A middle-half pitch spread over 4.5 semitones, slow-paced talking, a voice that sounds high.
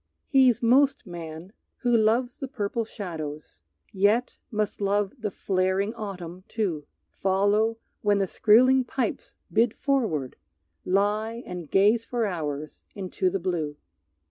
No: average, 4.0 semitones; slow, 125 wpm; high, 205 Hz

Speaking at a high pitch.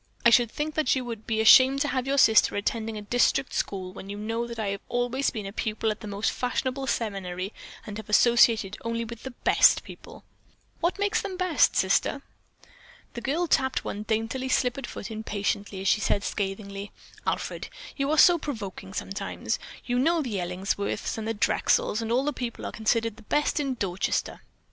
Yes: high, 230 Hz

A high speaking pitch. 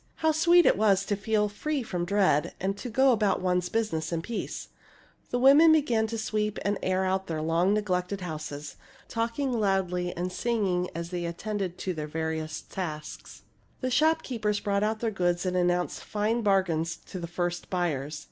Yes: high, 195 Hz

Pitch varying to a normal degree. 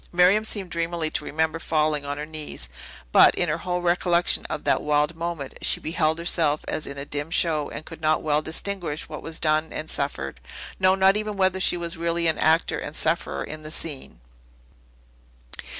No: narrow, 2.2 semitones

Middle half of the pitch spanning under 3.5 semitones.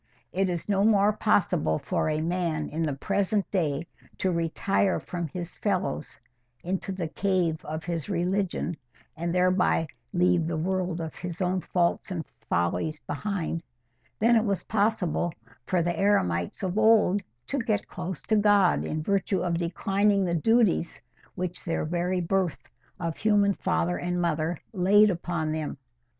Yes: average, 3.1 semitones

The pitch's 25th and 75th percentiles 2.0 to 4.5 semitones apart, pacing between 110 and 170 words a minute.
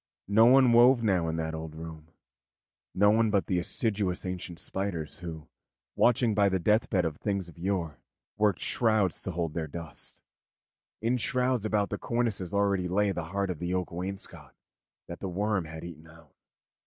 No: average, 4.0 semitones; average, 180 wpm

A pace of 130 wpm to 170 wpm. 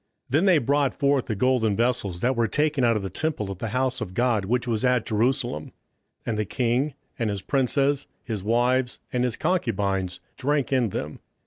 No: average, 195 wpm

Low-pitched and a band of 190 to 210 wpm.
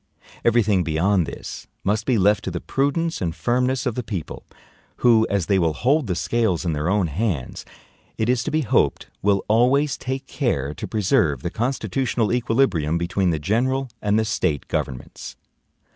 No: low, 105 Hz; average, 175 wpm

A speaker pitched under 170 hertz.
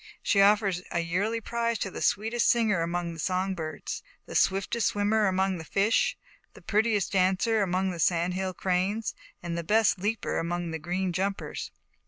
No: high, 190 Hz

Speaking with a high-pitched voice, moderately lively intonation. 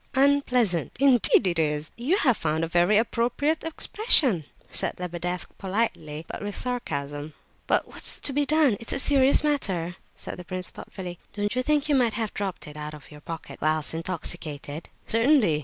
No: high, 200 Hz; wide, 8.1 semitones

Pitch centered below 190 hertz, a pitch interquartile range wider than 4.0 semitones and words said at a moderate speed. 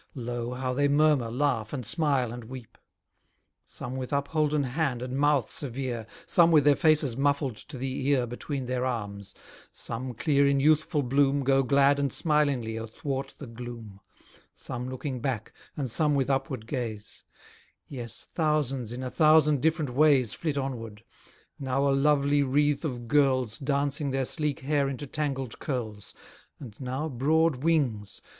No: low, 135 Hz; average, 2.9 semitones; average, 155 wpm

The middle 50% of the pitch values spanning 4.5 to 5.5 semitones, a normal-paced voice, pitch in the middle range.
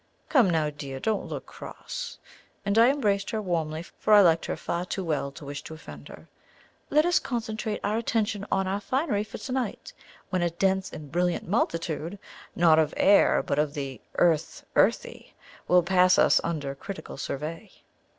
Yes: average, 5.1 semitones; average, 180 wpm; medium, 180 Hz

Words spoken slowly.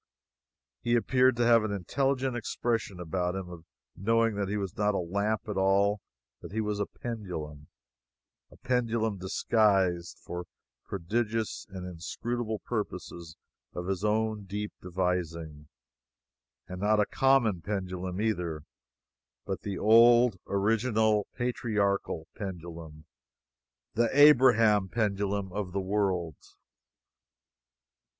Yes: slow, 115 wpm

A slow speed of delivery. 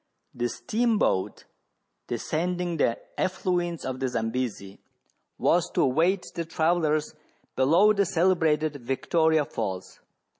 Yes: slow, 110 wpm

